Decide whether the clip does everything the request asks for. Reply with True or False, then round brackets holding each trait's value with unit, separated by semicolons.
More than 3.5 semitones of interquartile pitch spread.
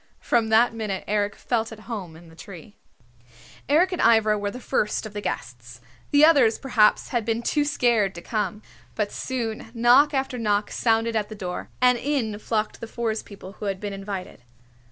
False (2.8 semitones)